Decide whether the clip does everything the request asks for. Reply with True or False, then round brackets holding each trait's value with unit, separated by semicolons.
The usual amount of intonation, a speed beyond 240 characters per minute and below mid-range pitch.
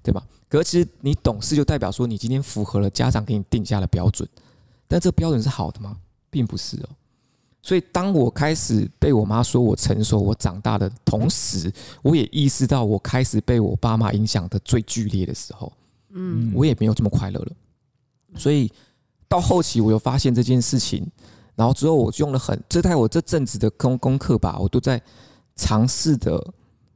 True (4.3 semitones; 285 characters per minute; 120 Hz)